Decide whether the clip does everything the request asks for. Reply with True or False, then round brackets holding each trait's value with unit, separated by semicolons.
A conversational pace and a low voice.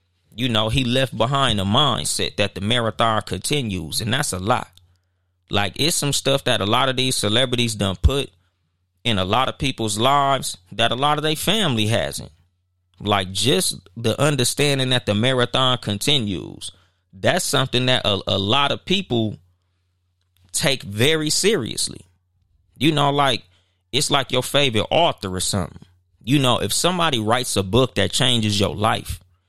True (165 wpm; 110 Hz)